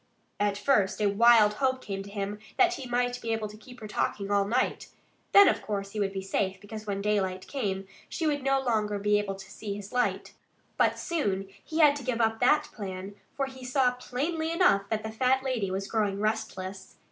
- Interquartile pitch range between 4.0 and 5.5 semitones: Yes, average, 4.3 semitones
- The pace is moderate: No, fast, 215 wpm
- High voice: Yes, high, 215 Hz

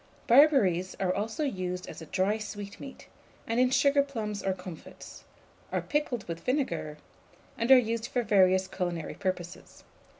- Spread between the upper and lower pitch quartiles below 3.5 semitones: No, wide, 5.4 semitones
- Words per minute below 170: Yes, average, 140 wpm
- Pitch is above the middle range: Yes, high, 205 Hz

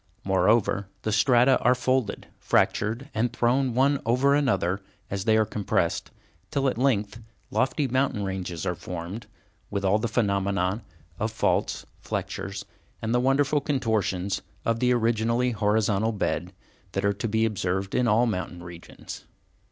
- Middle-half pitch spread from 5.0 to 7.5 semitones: No, average, 4.1 semitones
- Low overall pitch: Yes, low, 110 Hz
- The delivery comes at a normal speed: Yes, average, 145 wpm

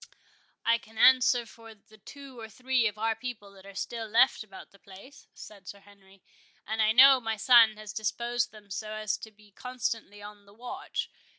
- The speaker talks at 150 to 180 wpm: No, average, 195 wpm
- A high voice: Yes, high, 220 Hz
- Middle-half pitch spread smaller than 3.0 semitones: Yes, narrow, 2.6 semitones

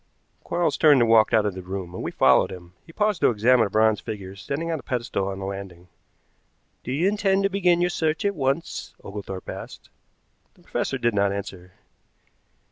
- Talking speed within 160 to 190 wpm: No, average, 200 wpm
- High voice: No, low, 110 Hz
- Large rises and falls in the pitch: Yes, wide, 8.8 semitones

